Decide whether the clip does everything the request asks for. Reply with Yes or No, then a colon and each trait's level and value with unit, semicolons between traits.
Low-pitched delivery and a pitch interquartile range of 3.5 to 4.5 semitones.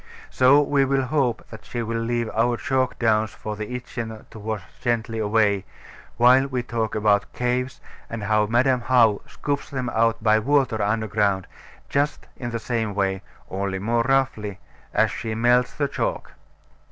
No: low, 115 Hz; average, 2.9 semitones